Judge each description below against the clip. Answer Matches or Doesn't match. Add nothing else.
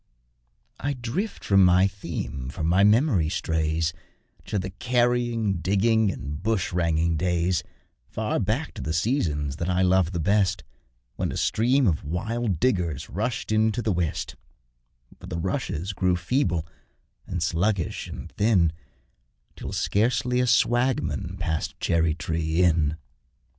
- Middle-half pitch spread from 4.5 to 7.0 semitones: Matches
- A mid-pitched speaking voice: Doesn't match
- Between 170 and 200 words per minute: Doesn't match